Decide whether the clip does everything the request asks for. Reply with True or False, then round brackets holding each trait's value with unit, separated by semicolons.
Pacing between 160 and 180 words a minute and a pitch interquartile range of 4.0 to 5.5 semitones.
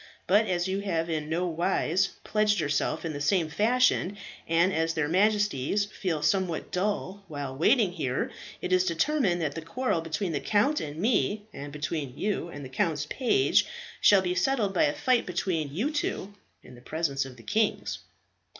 True (165 wpm; 4.8 semitones)